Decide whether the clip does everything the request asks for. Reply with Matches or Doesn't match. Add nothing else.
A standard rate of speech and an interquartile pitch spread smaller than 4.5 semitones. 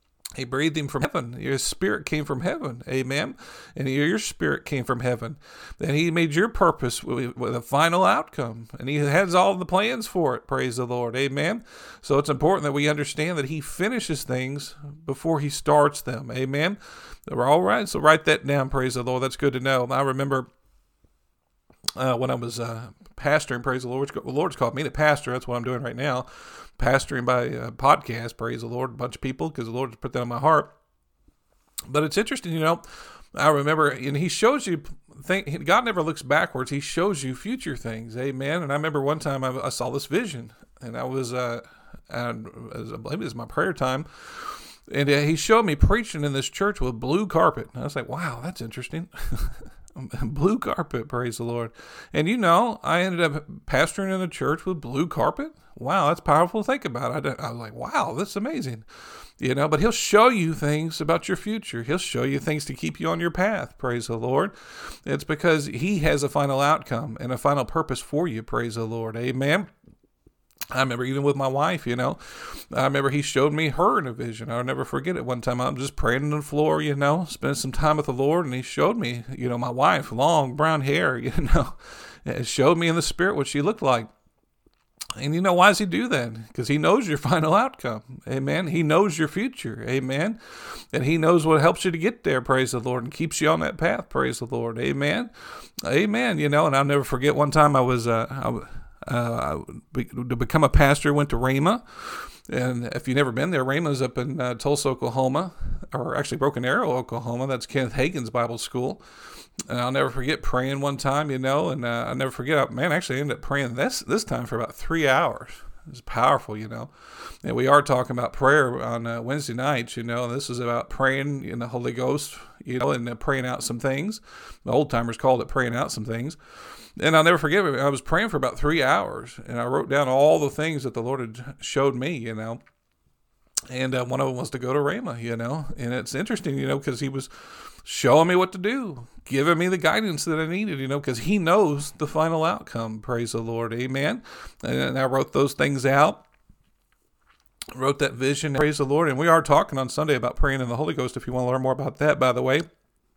Doesn't match